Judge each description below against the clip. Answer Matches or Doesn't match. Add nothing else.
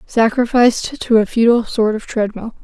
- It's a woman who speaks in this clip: Matches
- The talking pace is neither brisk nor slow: Matches